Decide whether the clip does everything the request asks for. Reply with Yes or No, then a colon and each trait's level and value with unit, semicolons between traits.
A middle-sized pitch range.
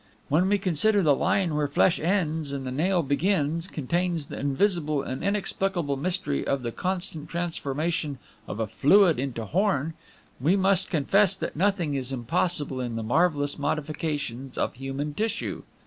Yes: average, 4.8 semitones